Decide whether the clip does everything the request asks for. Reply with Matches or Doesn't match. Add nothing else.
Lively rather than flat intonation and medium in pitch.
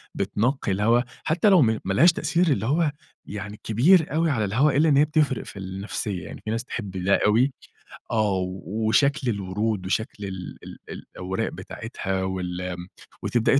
Doesn't match